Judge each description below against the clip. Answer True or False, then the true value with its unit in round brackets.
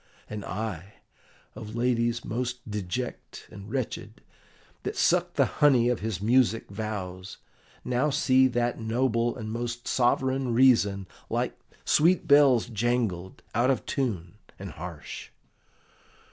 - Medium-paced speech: False (120 wpm)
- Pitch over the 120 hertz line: False (115 Hz)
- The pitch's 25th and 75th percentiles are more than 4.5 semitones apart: False (3.3 semitones)